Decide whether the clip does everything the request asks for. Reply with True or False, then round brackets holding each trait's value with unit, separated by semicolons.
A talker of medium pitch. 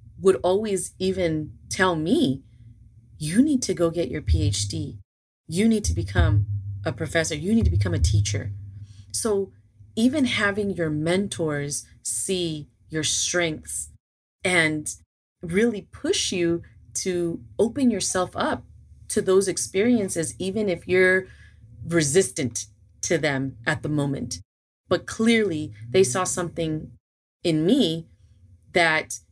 True (160 Hz)